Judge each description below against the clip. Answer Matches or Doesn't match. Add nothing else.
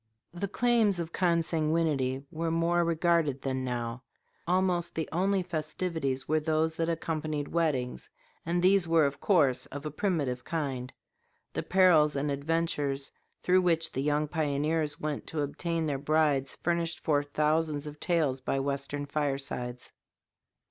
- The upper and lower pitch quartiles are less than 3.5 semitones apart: Matches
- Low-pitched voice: Doesn't match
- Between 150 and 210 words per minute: Doesn't match